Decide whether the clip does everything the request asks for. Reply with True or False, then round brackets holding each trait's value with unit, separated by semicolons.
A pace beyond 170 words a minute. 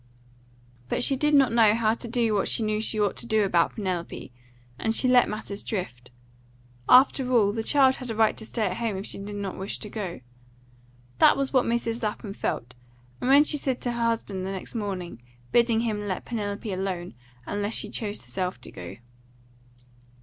True (195 wpm)